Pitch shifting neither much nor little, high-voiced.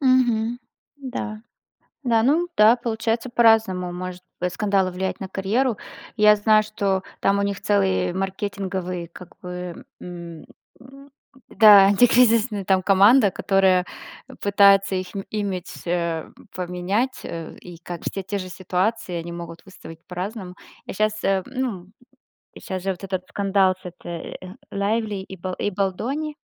Yes: average, 3.1 semitones; high, 195 Hz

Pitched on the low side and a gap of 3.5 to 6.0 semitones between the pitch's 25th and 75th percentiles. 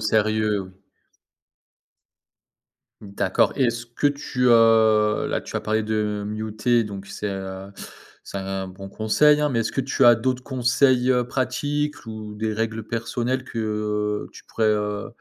No: low, 110 Hz; average, 2.8 semitones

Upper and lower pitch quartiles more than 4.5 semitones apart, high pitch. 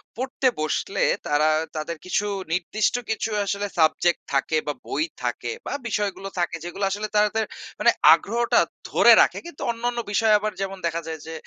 Yes: average, 4.9 semitones; high, 200 Hz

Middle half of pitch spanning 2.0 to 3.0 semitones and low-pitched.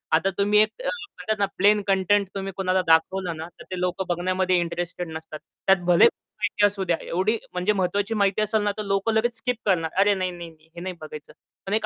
No: average, 2.7 semitones; high, 190 Hz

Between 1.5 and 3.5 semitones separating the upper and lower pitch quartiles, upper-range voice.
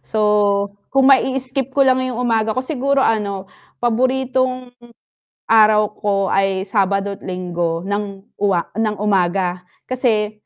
No: average, 4.4 semitones; high, 210 Hz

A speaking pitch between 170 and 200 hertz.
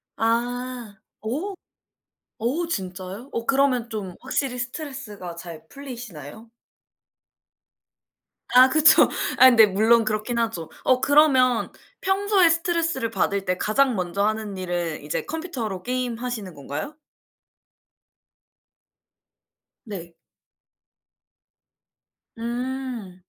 No: high, 235 Hz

